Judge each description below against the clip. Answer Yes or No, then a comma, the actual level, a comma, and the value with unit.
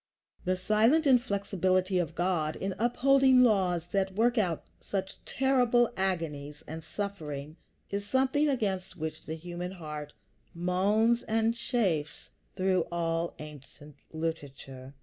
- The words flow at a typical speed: No, slow, 120 wpm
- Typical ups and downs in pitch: No, wide, 5.7 semitones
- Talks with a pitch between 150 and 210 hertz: Yes, medium, 185 Hz